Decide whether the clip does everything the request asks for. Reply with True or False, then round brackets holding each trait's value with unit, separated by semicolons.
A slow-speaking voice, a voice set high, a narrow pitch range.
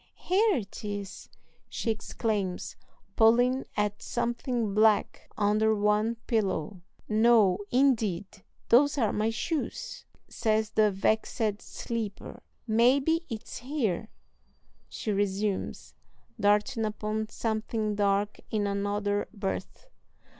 True (100 wpm; 215 Hz; 2.3 semitones)